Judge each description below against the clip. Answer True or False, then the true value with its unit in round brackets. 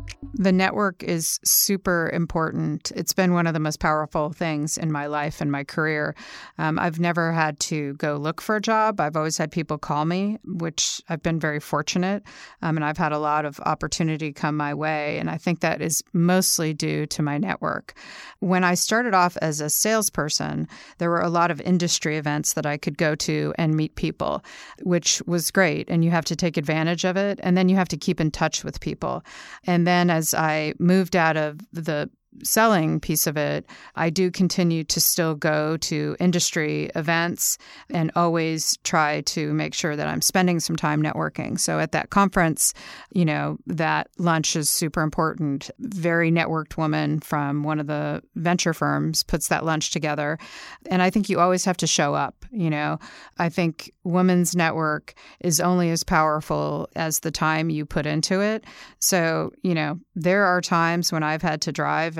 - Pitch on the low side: False (165 Hz)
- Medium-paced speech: True (190 wpm)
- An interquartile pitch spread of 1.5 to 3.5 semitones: True (2.6 semitones)